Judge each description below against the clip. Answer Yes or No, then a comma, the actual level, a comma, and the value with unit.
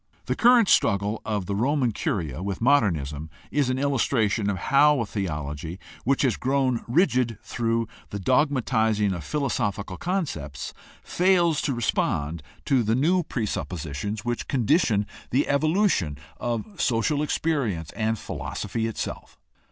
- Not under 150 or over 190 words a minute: No, slow, 135 wpm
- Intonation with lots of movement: Yes, wide, 5.9 semitones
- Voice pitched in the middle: No, low, 115 Hz